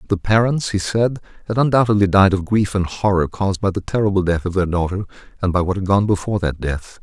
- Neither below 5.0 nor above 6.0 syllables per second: No, 6.2 syllables/s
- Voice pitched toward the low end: Yes, low, 100 Hz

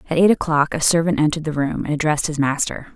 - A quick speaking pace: Yes, fast, 245 wpm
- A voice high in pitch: No, medium, 155 Hz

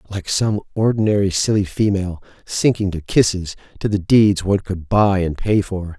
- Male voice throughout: Yes, male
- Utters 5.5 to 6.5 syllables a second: No, 5.0 syllables/s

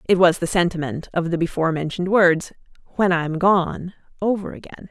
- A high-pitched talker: No, medium, 175 Hz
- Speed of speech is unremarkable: Yes, average, 170 wpm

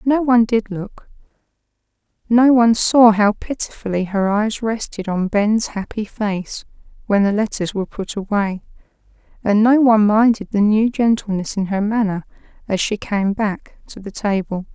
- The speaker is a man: No, female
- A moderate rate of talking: Yes, average, 160 wpm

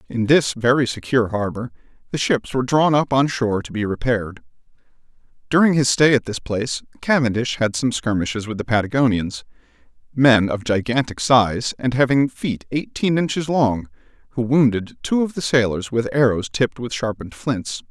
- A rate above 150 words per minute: Yes, average, 160 wpm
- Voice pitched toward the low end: Yes, low, 120 Hz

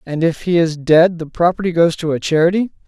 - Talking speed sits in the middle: No, fast, 230 wpm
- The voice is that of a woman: No, male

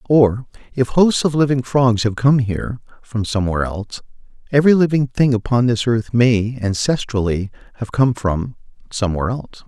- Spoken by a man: Yes, male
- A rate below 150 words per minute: Yes, slow, 135 wpm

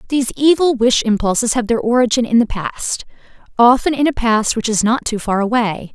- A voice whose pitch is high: Yes, high, 235 Hz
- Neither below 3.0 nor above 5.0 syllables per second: No, 5.4 syllables/s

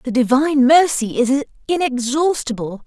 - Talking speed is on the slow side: Yes, slow, 105 wpm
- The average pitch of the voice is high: Yes, very high, 270 Hz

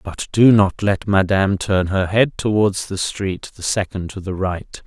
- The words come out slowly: No, average, 195 wpm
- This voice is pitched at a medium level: No, low, 100 Hz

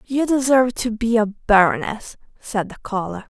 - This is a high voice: Yes, high, 225 Hz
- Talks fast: No, average, 160 wpm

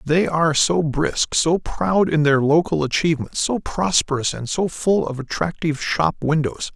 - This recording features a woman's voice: No, male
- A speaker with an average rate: Yes, average, 170 wpm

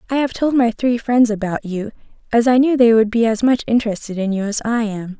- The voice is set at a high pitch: Yes, high, 230 Hz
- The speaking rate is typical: No, fast, 255 wpm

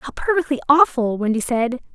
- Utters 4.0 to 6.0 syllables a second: Yes, 5.5 syllables/s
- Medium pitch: No, very high, 265 Hz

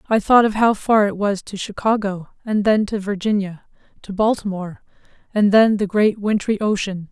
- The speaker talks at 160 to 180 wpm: Yes, average, 170 wpm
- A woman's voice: Yes, female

